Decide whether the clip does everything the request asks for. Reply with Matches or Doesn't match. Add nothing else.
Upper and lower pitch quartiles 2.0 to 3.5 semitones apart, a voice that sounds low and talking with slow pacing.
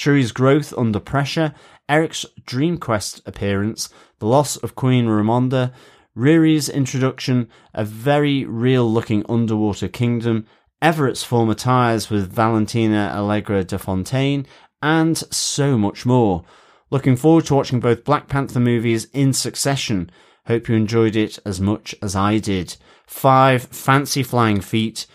Doesn't match